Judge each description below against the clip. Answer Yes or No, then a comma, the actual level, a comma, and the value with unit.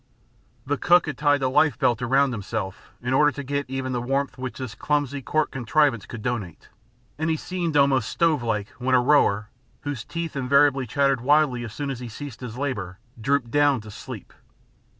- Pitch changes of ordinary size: Yes, average, 3.3 semitones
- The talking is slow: No, average, 190 wpm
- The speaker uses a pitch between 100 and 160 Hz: Yes, low, 135 Hz